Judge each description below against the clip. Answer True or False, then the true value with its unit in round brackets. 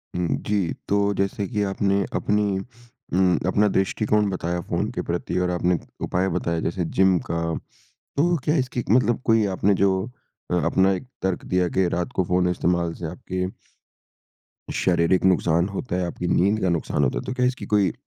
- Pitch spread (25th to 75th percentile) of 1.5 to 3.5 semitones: True (2.8 semitones)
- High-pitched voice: False (95 Hz)